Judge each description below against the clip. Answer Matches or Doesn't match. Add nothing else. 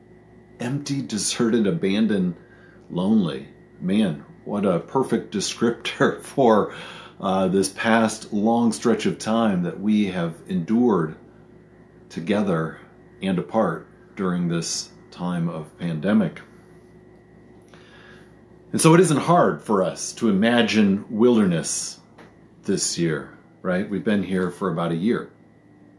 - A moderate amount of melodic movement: Doesn't match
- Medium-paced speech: Doesn't match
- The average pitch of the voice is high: Doesn't match